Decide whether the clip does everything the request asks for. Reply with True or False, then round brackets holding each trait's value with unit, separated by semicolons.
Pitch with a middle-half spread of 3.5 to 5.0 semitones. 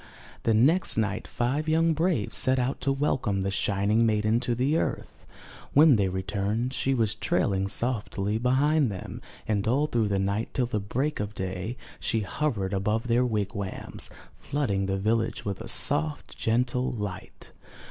True (4.5 semitones)